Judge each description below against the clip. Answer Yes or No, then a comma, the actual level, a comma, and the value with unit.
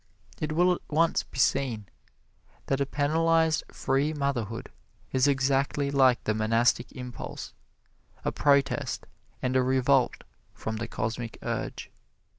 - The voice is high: No, low, 135 Hz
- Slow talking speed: Yes, slow, 125 wpm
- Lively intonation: No, average, 3.1 semitones